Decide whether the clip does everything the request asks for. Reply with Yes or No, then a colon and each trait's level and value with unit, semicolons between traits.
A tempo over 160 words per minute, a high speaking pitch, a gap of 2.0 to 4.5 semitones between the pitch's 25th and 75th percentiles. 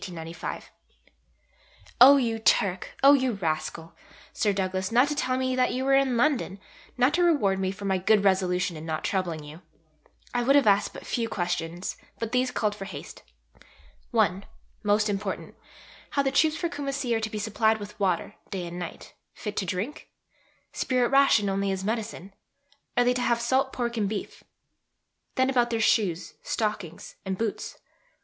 No: average, 170 wpm; high, 215 Hz; average, 4.9 semitones